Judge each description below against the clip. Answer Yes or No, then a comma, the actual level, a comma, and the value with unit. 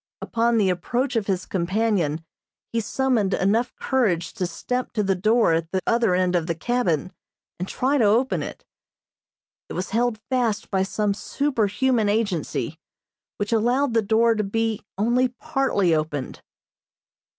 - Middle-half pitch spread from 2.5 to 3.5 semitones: No, average, 4.4 semitones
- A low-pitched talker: No, high, 215 Hz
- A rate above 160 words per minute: No, average, 150 wpm